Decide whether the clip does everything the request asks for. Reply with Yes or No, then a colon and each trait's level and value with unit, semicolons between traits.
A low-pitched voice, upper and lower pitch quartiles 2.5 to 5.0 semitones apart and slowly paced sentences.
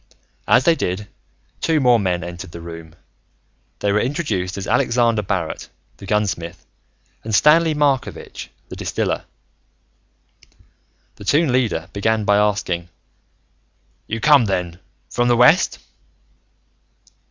No: low, 105 Hz; wide, 5.6 semitones; slow, 120 wpm